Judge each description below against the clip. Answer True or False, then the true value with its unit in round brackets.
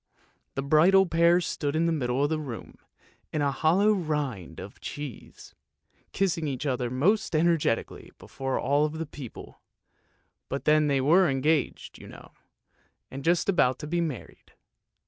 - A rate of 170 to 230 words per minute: False (160 wpm)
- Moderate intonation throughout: True (3.6 semitones)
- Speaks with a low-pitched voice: False (150 Hz)